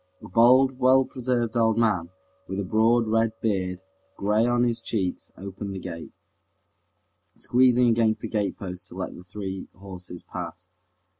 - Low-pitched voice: Yes, low, 110 Hz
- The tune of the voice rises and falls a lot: No, average, 3.9 semitones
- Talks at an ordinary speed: Yes, average, 150 wpm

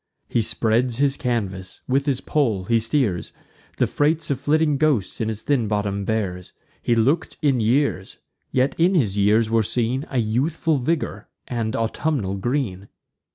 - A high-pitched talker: No, low, 120 Hz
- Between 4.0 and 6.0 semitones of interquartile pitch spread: Yes, average, 4.9 semitones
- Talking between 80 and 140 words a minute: No, average, 155 wpm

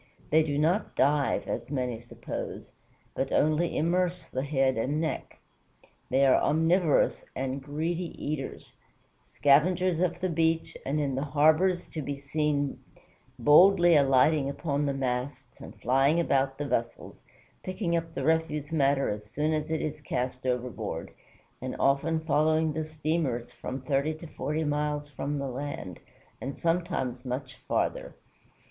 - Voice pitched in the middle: Yes, medium, 145 Hz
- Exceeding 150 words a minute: No, average, 145 wpm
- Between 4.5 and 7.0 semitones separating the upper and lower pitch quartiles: No, average, 3.0 semitones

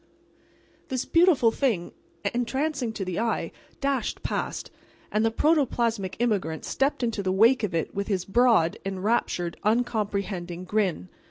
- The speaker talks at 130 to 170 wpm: Yes, slow, 135 wpm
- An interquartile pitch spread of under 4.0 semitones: No, average, 4.4 semitones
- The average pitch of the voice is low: No, high, 220 Hz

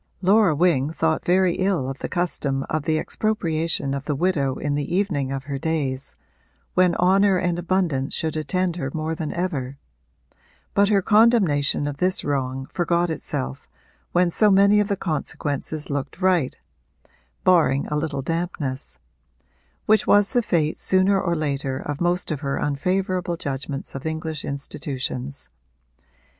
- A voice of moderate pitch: Yes, medium, 160 Hz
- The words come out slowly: No, average, 150 wpm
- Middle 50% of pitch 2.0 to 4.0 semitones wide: No, average, 4.6 semitones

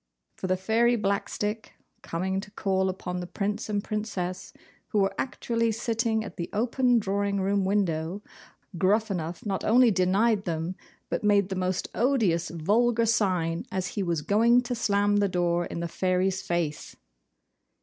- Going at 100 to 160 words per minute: Yes, average, 155 wpm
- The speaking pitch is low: No, high, 200 Hz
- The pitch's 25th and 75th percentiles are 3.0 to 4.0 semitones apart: Yes, average, 3.3 semitones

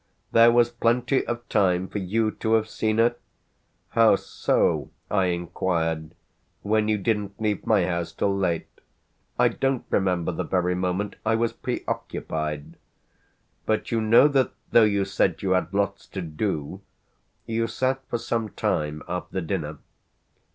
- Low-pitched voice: Yes, low, 100 Hz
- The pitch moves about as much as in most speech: Yes, average, 4.0 semitones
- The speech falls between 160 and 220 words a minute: No, average, 150 wpm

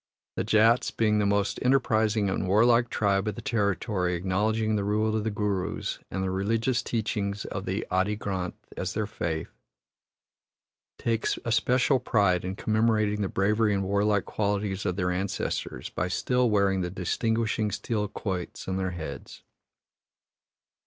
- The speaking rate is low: No, average, 150 wpm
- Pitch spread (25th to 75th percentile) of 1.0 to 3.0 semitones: Yes, narrow, 2.5 semitones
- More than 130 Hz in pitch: No, low, 105 Hz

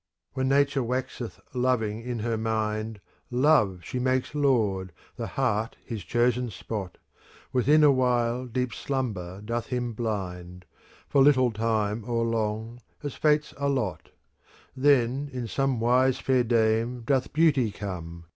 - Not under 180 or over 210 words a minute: No, slow, 135 wpm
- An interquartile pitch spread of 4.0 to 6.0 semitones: No, average, 3.2 semitones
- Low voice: Yes, low, 120 Hz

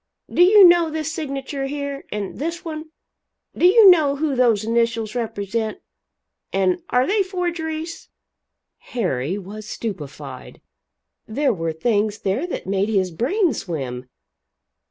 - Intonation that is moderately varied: No, wide, 8.0 semitones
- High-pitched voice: Yes, high, 245 Hz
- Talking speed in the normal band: No, slow, 130 wpm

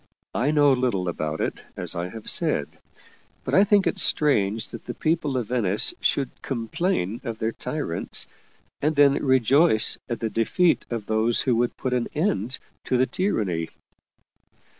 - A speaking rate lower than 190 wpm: Yes, average, 160 wpm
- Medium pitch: No, low, 125 Hz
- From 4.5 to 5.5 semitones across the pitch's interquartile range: Yes, average, 5.1 semitones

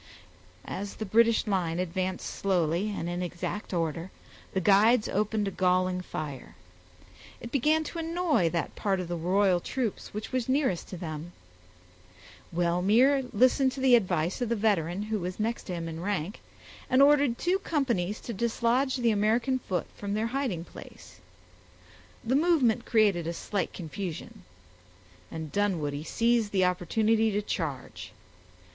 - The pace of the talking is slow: No, average, 150 wpm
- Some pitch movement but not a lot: Yes, average, 5.0 semitones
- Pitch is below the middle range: No, high, 205 Hz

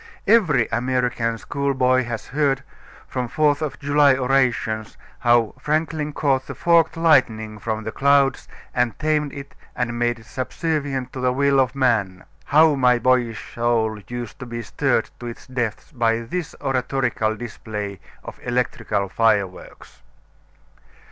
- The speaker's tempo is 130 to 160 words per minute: Yes, average, 140 wpm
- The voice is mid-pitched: No, low, 125 Hz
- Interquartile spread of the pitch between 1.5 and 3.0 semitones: No, average, 3.4 semitones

